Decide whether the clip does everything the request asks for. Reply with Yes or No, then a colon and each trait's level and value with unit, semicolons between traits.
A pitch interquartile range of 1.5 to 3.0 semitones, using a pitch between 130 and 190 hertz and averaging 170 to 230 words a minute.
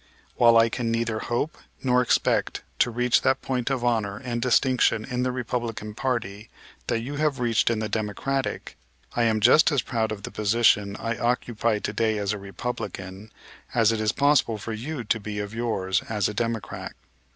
No: narrow, 2.5 semitones; low, 115 Hz; average, 185 wpm